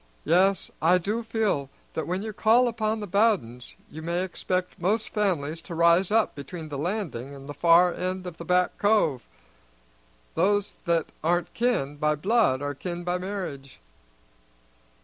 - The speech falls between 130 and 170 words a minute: Yes, average, 160 wpm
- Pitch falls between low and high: Yes, medium, 180 Hz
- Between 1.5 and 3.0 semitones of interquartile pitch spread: No, average, 4.6 semitones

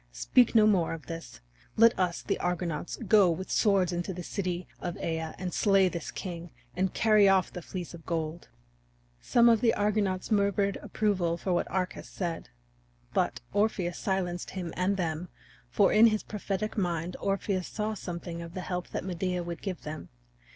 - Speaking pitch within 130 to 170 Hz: No, medium, 185 Hz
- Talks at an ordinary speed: Yes, average, 175 wpm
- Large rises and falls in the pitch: No, average, 2.7 semitones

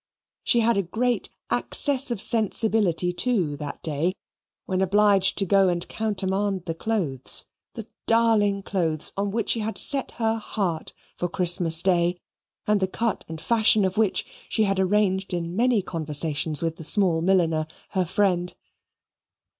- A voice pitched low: No, high, 190 Hz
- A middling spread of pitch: Yes, average, 4.1 semitones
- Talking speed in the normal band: Yes, average, 155 wpm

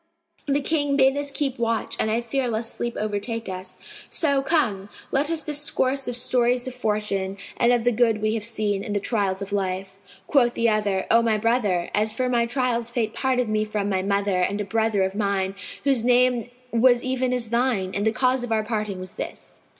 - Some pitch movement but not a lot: Yes, average, 3.6 semitones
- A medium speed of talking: No, fast, 210 wpm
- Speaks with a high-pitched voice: Yes, high, 230 Hz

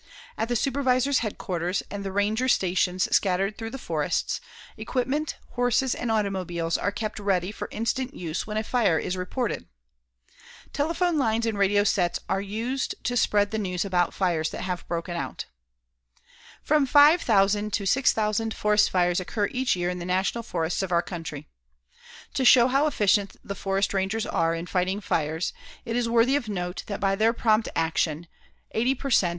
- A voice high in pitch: Yes, high, 205 Hz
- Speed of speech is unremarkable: Yes, average, 175 wpm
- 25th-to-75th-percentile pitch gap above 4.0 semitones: Yes, average, 4.7 semitones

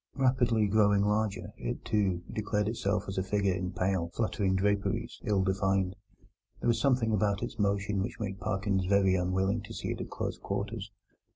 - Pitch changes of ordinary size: No, narrow, 2.1 semitones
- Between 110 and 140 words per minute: No, average, 175 wpm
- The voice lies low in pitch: Yes, low, 100 Hz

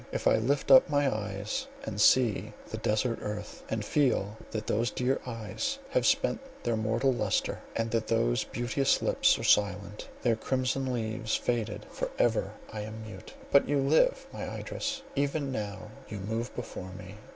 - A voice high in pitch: No, low, 115 Hz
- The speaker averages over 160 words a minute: Yes, average, 170 wpm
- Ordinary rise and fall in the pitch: Yes, average, 4.0 semitones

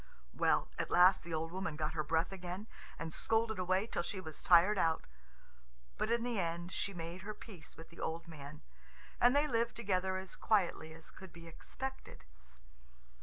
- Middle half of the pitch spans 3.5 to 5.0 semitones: Yes, average, 4.2 semitones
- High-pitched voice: No, medium, 180 Hz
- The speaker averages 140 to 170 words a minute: No, average, 180 wpm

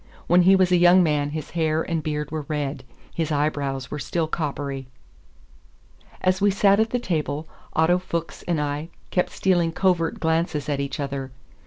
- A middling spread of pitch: Yes, average, 3.2 semitones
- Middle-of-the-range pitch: Yes, medium, 160 Hz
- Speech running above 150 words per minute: Yes, average, 175 wpm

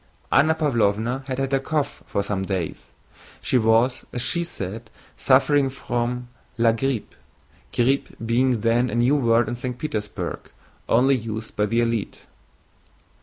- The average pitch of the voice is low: Yes, low, 120 Hz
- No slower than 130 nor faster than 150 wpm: Yes, average, 145 wpm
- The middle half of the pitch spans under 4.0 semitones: Yes, average, 3.0 semitones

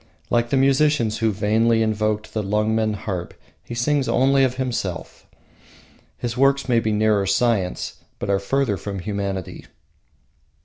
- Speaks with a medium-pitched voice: No, low, 110 Hz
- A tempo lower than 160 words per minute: Yes, average, 140 wpm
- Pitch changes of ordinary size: Yes, average, 3.5 semitones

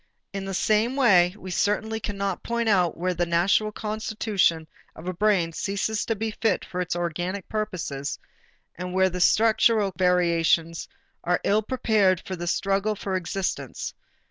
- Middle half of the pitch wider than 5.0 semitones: No, average, 3.4 semitones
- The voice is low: No, high, 195 Hz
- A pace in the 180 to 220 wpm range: No, average, 155 wpm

